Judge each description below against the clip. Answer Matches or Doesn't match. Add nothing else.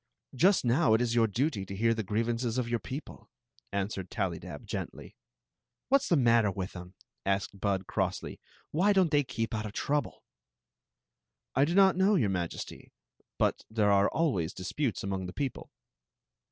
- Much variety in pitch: Matches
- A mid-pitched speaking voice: Doesn't match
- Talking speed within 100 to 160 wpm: Doesn't match